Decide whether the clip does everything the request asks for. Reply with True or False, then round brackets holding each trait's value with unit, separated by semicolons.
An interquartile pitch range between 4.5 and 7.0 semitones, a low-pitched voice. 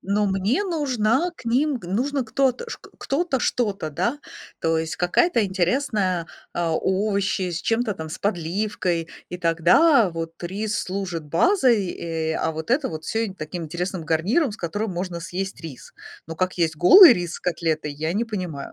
False (5.6 semitones; 190 Hz)